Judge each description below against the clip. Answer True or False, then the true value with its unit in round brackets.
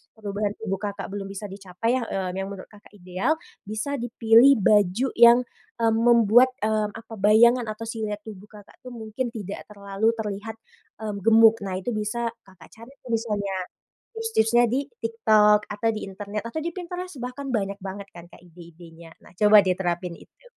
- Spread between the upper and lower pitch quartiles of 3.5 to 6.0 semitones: False (2.7 semitones)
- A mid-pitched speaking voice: False (215 Hz)